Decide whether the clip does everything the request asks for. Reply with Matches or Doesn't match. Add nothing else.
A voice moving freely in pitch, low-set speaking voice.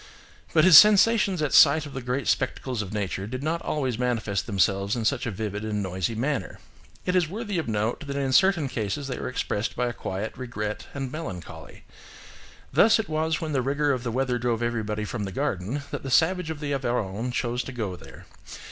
Matches